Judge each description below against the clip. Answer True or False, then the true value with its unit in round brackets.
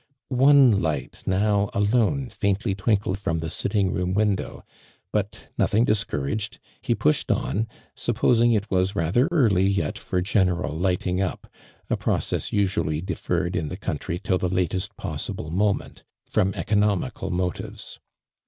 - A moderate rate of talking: True (145 wpm)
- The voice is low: True (95 Hz)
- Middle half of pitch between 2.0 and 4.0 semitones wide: True (2.8 semitones)